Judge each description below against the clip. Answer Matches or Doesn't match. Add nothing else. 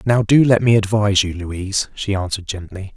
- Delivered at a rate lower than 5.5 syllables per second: Doesn't match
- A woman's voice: Doesn't match